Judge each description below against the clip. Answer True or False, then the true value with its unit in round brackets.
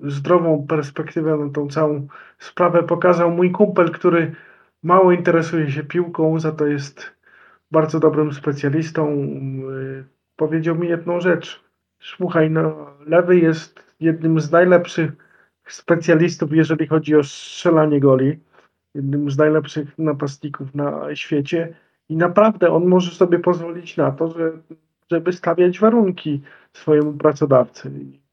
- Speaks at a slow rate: False (125 wpm)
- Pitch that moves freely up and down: False (2.4 semitones)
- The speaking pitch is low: False (160 Hz)